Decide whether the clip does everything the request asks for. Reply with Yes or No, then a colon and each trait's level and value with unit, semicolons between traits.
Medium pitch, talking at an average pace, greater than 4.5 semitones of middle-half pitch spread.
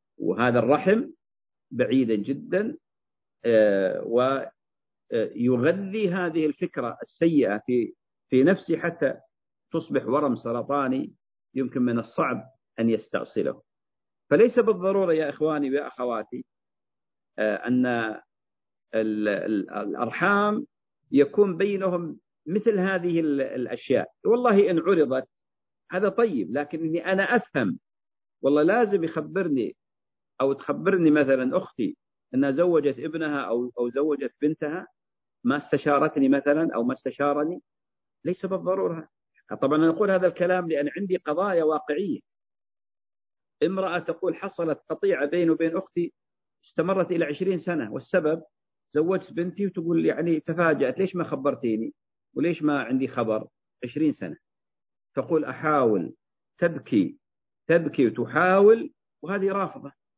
Yes: medium, 160 Hz; average, 105 wpm; average, 5.3 semitones